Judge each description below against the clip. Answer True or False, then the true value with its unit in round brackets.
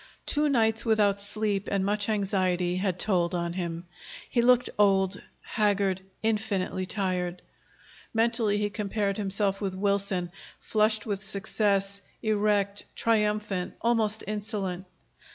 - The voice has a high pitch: True (200 Hz)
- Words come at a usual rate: False (115 wpm)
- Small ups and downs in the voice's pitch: True (2.0 semitones)